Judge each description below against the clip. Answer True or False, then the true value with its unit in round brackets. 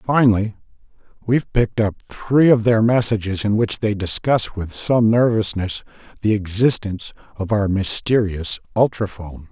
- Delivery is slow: True (130 wpm)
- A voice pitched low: True (105 Hz)